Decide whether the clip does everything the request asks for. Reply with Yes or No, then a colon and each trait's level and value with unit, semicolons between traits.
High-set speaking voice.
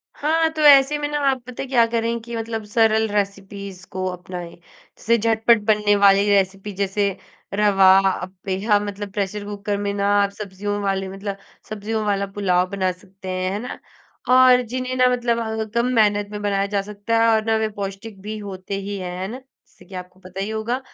Yes: high, 205 Hz